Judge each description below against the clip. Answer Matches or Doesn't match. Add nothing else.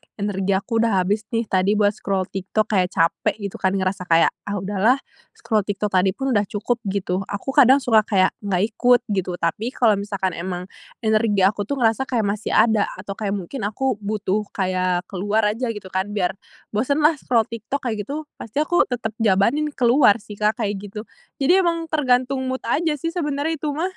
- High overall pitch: Matches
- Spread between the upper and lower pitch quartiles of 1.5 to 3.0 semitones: Doesn't match